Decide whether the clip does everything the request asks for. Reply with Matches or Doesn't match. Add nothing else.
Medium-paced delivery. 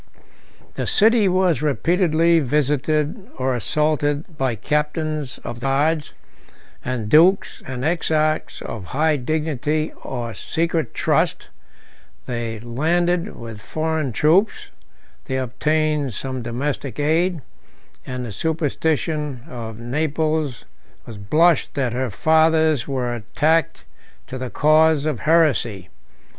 Doesn't match